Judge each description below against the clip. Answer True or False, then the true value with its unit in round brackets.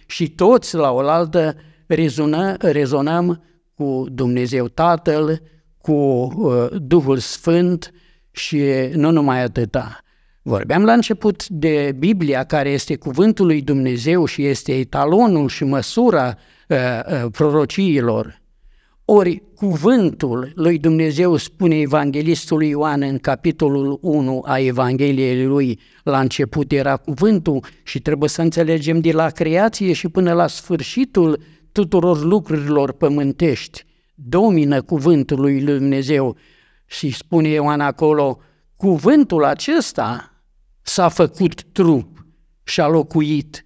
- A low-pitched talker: False (155 Hz)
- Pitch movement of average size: True (3.7 semitones)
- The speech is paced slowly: True (105 wpm)